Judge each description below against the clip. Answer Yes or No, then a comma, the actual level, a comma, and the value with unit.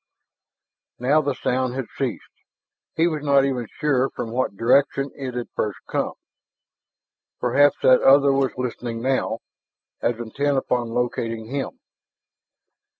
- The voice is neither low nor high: No, low, 130 Hz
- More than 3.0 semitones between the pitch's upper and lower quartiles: No, narrow, 2.5 semitones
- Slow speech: Yes, slow, 130 wpm